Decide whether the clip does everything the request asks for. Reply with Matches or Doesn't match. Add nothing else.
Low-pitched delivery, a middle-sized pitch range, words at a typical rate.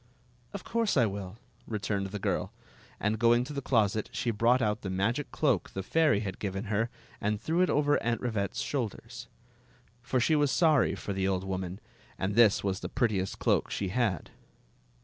Matches